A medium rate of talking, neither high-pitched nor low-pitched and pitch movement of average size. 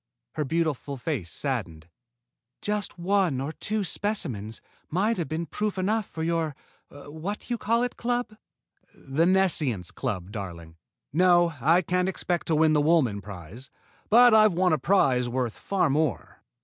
No: average, 150 wpm; medium, 160 Hz; wide, 6.8 semitones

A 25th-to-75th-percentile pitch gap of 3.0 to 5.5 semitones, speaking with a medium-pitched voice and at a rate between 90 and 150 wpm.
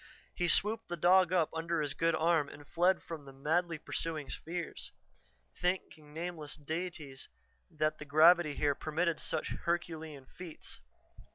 No: narrow, 2.4 semitones; medium, 165 Hz; average, 145 wpm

